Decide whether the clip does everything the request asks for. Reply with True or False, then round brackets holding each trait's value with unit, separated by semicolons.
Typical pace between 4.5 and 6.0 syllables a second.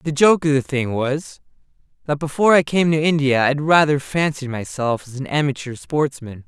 True (5.2 syllables/s)